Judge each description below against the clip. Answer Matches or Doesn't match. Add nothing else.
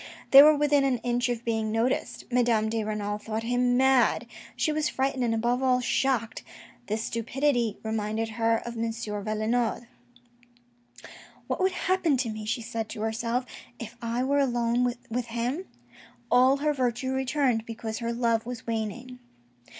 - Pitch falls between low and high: Doesn't match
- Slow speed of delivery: Doesn't match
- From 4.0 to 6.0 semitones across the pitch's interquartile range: Doesn't match